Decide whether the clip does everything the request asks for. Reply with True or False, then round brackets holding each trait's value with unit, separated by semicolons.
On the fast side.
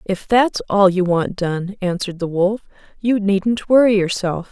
False (175 wpm)